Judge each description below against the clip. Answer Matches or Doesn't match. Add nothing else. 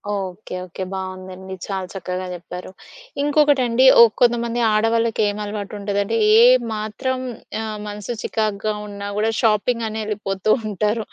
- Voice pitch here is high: Matches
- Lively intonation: Doesn't match